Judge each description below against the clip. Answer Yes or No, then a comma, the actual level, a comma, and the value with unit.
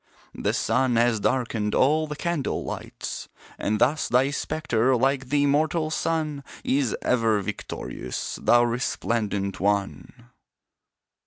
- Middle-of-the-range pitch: No, low, 125 Hz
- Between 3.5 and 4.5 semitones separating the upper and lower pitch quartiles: Yes, average, 4.2 semitones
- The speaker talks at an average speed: No, slow, 115 wpm